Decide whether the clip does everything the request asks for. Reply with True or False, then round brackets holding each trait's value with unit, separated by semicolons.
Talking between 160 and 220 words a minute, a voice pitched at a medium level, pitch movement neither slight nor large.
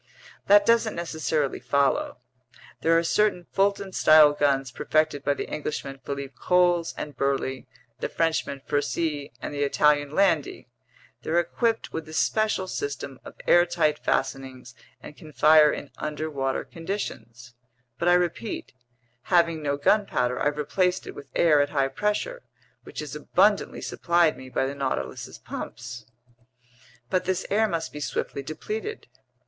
False (145 wpm; 155 Hz; 4.1 semitones)